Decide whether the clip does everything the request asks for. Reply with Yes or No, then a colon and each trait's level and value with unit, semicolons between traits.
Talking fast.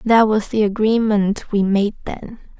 No: average, 160 wpm